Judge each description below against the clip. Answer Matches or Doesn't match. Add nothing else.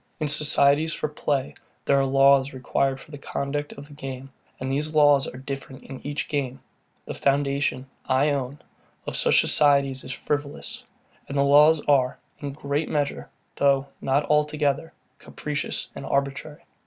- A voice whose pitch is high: Doesn't match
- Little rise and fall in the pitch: Matches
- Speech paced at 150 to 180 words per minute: Matches